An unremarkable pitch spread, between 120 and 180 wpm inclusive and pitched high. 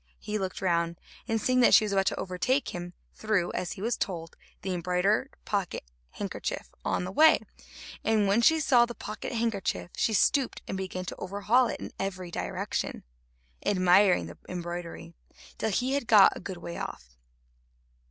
Yes: average, 3.9 semitones; average, 170 wpm; high, 195 Hz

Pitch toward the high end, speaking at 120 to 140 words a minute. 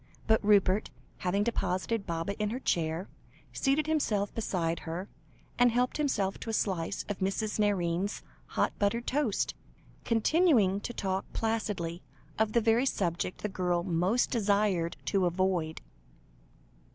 Yes: high, 200 Hz; slow, 135 wpm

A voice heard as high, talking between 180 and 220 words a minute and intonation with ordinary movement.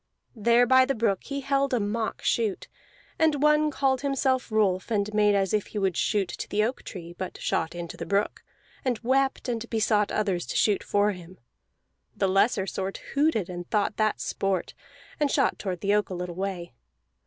Yes: high, 210 Hz; average, 190 wpm; average, 5.0 semitones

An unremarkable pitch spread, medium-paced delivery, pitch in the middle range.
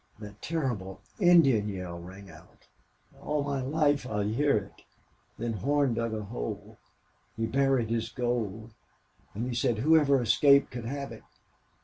No: average, 4.9 semitones; average, 145 wpm; low, 120 Hz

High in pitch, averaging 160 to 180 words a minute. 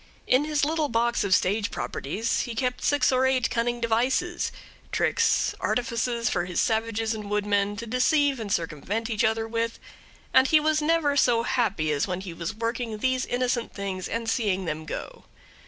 Yes: high, 230 Hz; average, 175 wpm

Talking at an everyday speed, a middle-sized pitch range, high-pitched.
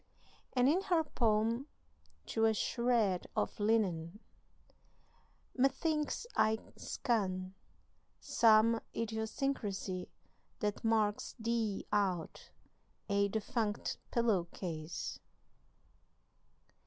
No: slow, 80 wpm; average, 3.0 semitones; high, 220 Hz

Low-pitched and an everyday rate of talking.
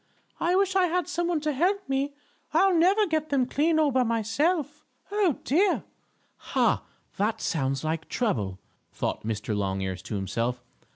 No: very high, 280 Hz; average, 160 wpm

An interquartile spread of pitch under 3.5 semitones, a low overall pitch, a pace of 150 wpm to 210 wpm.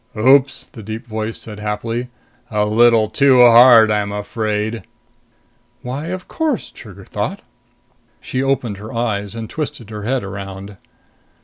No: average, 3.0 semitones; low, 110 Hz; slow, 135 wpm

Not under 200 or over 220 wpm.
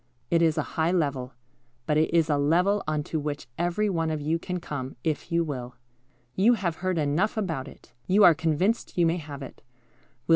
Yes: fast, 205 wpm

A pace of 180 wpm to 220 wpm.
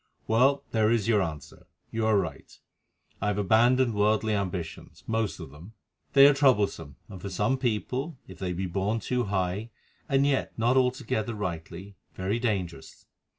No: average, 155 wpm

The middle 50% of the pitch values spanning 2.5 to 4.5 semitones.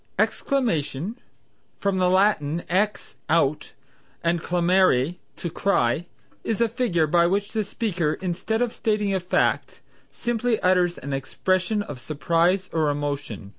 No: average, 4.9 semitones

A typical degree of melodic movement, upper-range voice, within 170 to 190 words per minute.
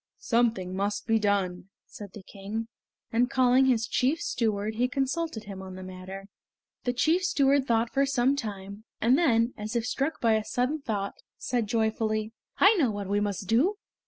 Yes: average, 4.2 semitones; high, 225 Hz; average, 180 wpm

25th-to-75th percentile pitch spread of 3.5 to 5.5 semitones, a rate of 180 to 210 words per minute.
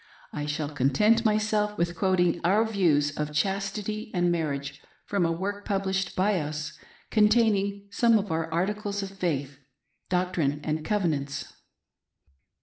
No: average, 5.1 semitones; slow, 135 wpm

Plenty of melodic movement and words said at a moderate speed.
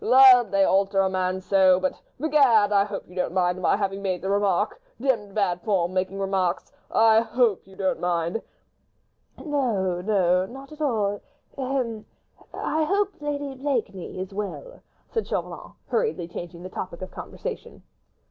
Yes: wide, 5.7 semitones; average, 155 wpm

